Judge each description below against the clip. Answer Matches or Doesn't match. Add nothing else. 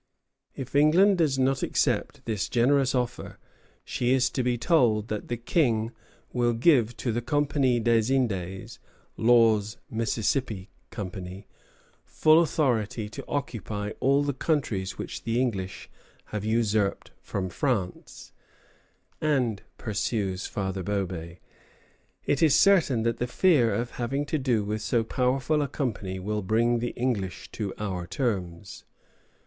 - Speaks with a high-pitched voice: Doesn't match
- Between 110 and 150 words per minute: Matches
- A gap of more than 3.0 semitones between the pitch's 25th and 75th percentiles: Matches